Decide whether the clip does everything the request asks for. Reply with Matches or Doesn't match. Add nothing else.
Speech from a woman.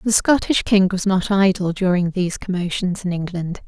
Matches